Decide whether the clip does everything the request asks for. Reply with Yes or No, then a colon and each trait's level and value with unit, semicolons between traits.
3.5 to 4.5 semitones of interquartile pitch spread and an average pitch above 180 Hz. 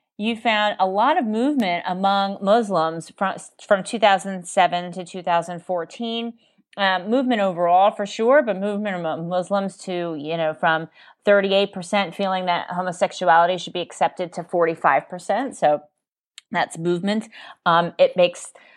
No: average, 2.9 semitones; high, 190 Hz